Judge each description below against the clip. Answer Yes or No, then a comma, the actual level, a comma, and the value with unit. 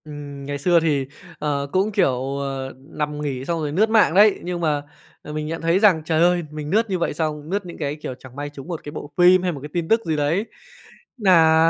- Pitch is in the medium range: Yes, medium, 155 Hz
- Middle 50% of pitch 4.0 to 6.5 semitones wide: No, average, 3.5 semitones